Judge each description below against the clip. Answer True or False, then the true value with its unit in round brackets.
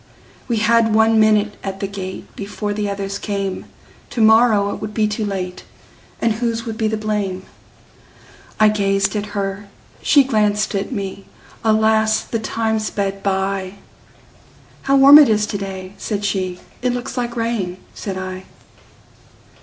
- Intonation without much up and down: True (2.1 semitones)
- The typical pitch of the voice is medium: False (210 Hz)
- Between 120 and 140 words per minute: True (135 wpm)